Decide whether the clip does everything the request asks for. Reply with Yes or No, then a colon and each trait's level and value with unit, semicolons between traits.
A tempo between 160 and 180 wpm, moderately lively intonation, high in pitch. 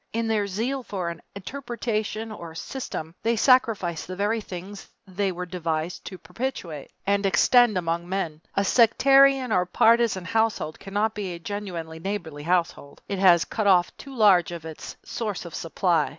Yes: average, 170 wpm; average, 4.5 semitones; high, 195 Hz